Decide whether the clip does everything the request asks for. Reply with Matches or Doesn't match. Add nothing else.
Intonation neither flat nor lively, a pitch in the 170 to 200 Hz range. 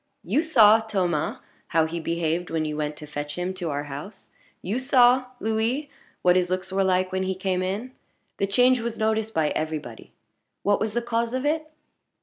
Doesn't match